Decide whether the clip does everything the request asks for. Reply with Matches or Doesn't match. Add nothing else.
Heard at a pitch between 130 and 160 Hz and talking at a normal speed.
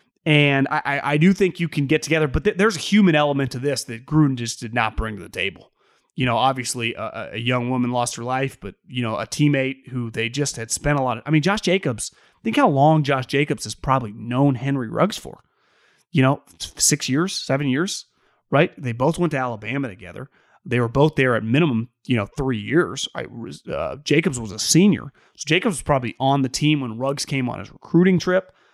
Doesn't match